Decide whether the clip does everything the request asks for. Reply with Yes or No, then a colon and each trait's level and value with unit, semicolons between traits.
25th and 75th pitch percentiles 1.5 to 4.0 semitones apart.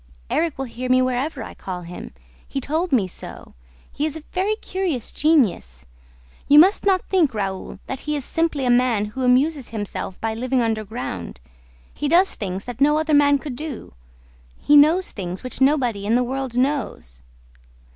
No: average, 5.3 semitones